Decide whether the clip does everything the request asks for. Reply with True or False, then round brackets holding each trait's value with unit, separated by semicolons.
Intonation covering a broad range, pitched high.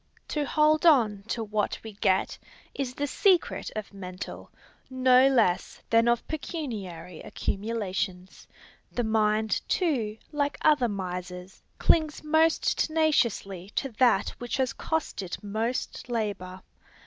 True (6.3 semitones; 230 Hz)